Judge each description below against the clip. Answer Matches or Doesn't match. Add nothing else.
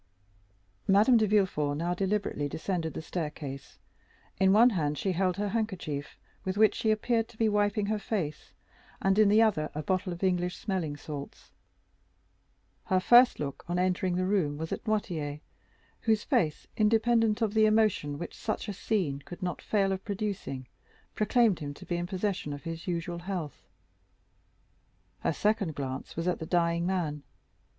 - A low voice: Doesn't match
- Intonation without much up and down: Doesn't match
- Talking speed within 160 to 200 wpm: Matches